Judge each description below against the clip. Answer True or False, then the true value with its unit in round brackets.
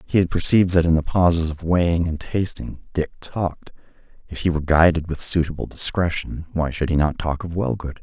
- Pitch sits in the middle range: False (85 Hz)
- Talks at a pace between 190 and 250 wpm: True (200 wpm)